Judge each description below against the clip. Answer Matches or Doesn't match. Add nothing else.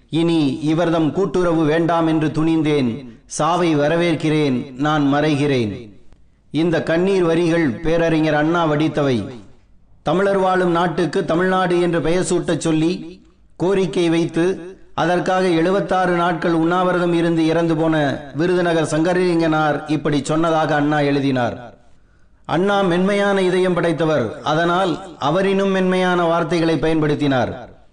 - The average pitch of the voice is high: Doesn't match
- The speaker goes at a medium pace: Matches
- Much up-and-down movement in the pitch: Doesn't match